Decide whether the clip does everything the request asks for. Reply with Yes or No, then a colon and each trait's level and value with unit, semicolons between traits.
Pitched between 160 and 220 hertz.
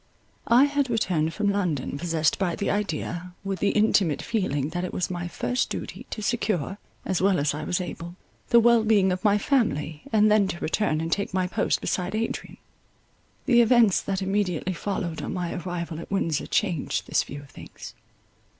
Yes: high, 190 Hz